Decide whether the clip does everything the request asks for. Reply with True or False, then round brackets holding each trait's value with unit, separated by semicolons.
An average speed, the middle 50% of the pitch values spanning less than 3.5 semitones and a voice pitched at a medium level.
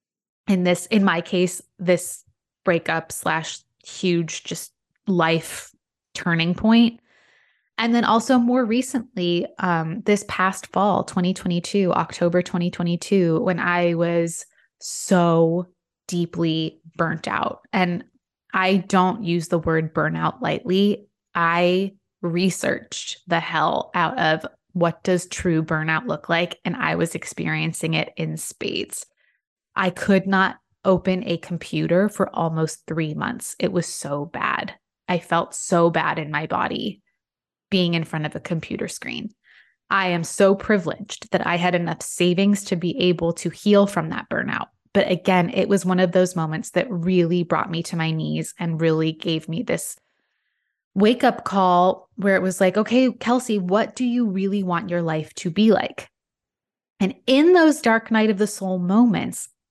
True (155 wpm; 2.9 semitones; 180 Hz)